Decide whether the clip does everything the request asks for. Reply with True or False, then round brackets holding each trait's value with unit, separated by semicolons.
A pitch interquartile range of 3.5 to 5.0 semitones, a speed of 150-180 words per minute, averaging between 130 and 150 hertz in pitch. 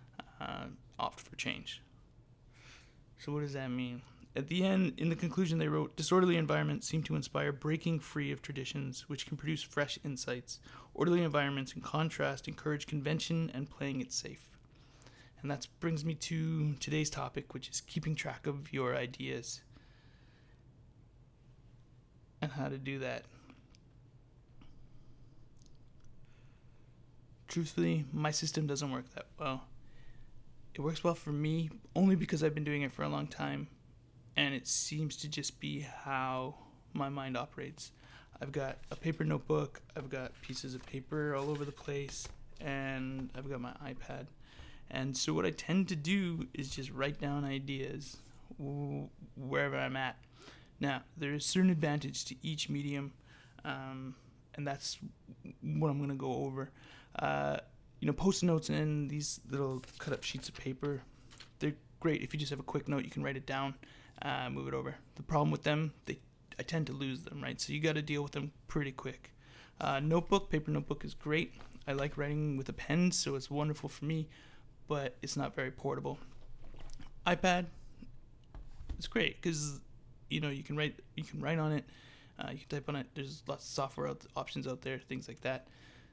False (3.0 semitones; 170 wpm; 140 Hz)